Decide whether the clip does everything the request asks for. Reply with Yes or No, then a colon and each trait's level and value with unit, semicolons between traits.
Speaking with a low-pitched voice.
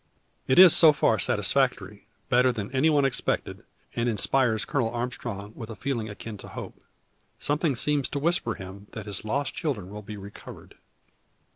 Yes: low, 120 Hz